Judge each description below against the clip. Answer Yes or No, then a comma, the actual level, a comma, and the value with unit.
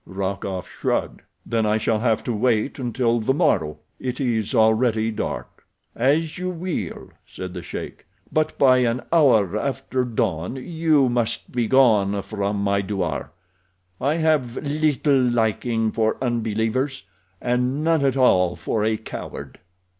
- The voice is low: Yes, low, 120 Hz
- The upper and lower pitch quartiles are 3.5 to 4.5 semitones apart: Yes, average, 3.9 semitones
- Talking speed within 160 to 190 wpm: No, average, 140 wpm